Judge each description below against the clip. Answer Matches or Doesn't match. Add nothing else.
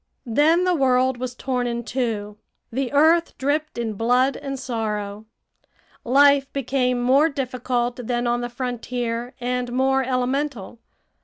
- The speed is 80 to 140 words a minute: Matches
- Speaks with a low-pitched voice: Doesn't match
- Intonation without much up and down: Matches